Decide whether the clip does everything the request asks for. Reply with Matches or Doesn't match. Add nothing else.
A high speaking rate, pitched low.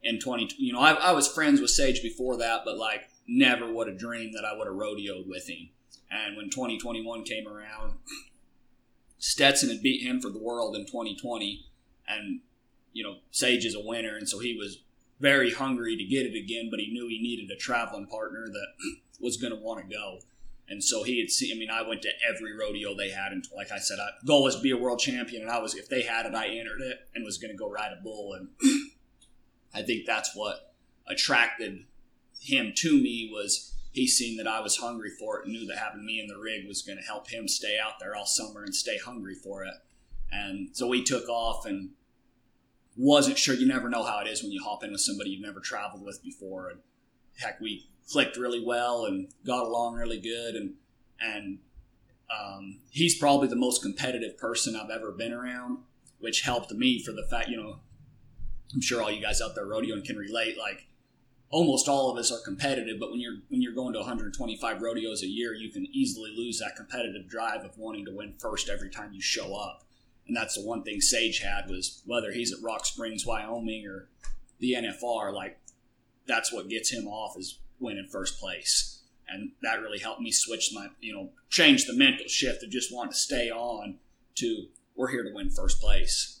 Matches